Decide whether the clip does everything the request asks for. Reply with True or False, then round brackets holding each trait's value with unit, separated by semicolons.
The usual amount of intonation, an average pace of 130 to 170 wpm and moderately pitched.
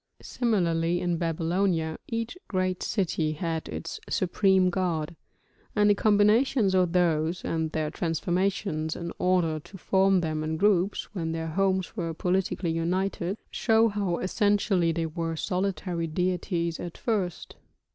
True (3.0 semitones; 135 wpm; 180 Hz)